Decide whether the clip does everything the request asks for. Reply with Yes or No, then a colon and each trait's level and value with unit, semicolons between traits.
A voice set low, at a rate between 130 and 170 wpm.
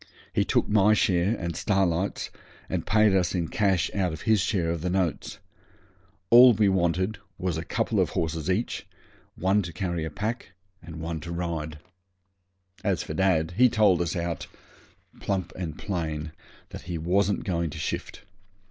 Yes: very low, 90 Hz; average, 165 wpm